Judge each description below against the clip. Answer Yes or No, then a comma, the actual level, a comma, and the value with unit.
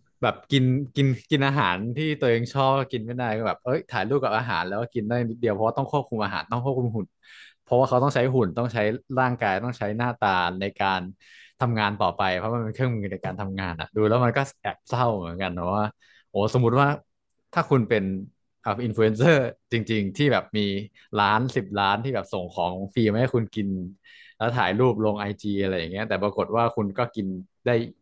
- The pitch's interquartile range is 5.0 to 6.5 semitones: No, average, 3.7 semitones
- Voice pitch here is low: Yes, low, 115 Hz